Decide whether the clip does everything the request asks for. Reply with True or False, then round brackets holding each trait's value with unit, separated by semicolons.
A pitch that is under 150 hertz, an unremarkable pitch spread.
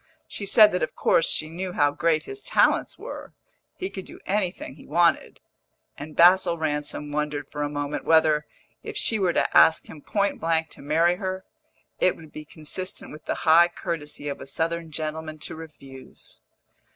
False (160 Hz; 3.1 semitones)